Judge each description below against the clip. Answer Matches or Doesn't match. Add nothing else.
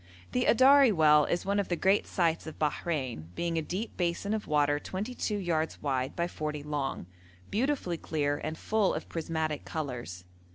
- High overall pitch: Doesn't match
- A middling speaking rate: Matches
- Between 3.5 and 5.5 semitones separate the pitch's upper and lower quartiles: Matches